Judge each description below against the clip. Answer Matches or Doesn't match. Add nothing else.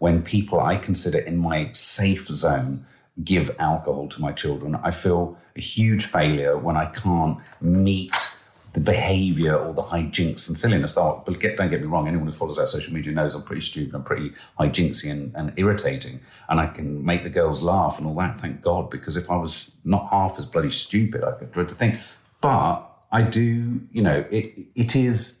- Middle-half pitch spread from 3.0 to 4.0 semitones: Doesn't match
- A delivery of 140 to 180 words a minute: Doesn't match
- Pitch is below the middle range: Matches